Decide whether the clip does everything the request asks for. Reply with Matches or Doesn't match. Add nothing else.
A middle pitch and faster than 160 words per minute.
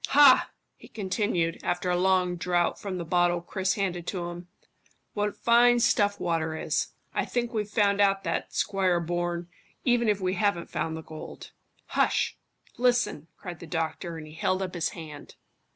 Matches